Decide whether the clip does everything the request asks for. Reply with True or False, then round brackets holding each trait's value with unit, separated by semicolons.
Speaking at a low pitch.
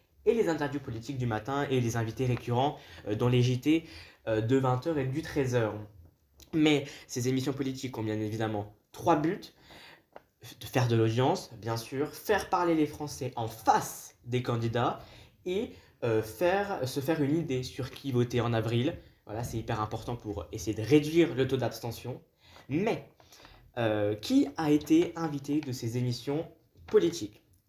True (125 Hz)